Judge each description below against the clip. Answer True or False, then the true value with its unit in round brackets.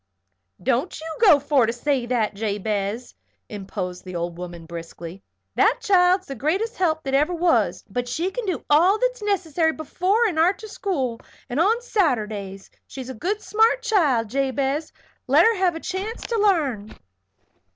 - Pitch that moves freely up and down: True (8.9 semitones)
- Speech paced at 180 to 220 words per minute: False (160 wpm)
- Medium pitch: False (300 Hz)